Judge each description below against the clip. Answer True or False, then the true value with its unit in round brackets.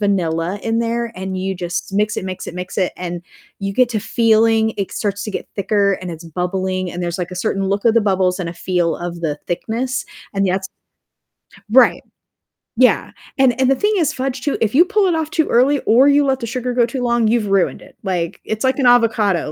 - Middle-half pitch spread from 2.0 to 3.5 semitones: False (4.9 semitones)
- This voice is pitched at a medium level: False (210 Hz)